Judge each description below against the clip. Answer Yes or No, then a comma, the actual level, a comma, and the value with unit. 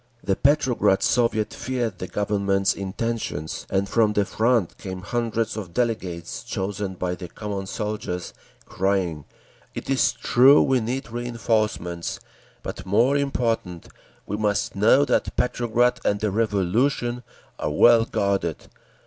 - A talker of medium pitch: No, low, 105 Hz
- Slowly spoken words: Yes, slow, 130 wpm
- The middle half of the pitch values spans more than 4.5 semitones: No, average, 3.8 semitones